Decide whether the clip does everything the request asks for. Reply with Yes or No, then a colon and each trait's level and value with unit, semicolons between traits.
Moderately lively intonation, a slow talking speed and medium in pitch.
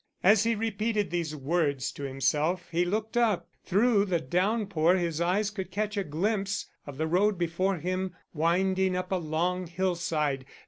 No: average, 3.4 semitones; average, 165 wpm; medium, 180 Hz